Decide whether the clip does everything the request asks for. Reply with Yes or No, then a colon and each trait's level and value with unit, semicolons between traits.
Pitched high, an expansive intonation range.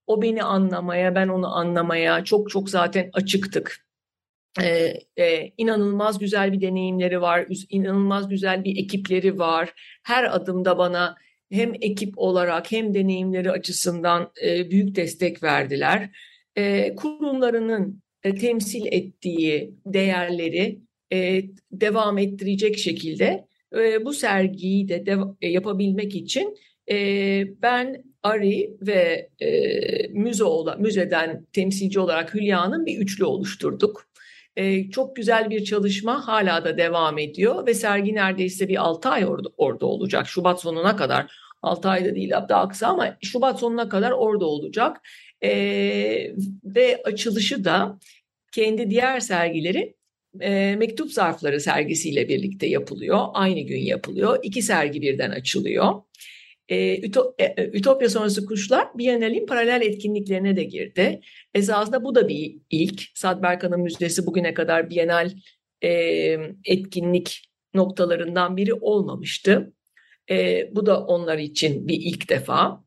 No: high, 195 Hz; average, 3.8 semitones